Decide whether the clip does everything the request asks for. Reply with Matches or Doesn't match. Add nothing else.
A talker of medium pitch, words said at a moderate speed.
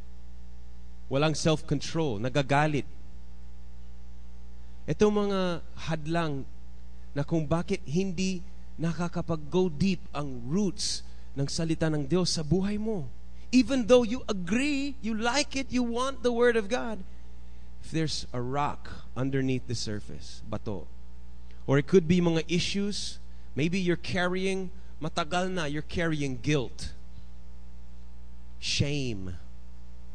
Doesn't match